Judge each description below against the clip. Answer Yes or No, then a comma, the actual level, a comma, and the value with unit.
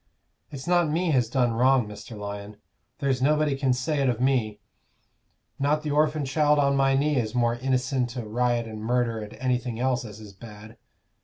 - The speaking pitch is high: No, low, 125 Hz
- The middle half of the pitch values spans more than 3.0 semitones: Yes, average, 3.5 semitones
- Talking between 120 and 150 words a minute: No, average, 185 wpm